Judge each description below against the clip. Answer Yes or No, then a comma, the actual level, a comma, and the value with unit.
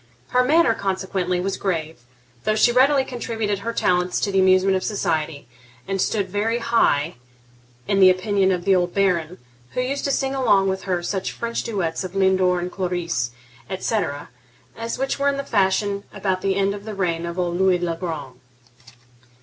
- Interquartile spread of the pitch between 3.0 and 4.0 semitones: Yes, average, 3.3 semitones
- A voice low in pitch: No, high, 190 Hz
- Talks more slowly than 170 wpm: No, average, 175 wpm